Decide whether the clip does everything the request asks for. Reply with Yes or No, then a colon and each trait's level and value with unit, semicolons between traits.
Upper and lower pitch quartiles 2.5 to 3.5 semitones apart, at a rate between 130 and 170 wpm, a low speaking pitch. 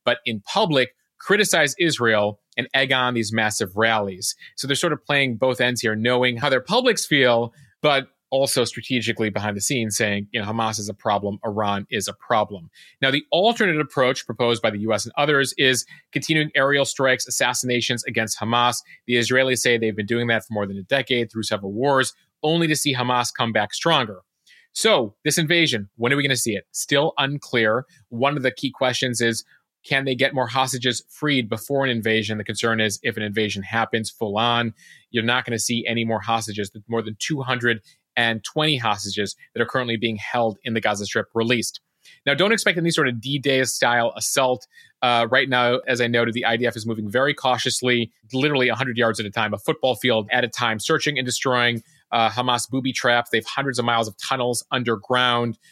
No: average, 3.0 semitones; average, 200 wpm; low, 120 Hz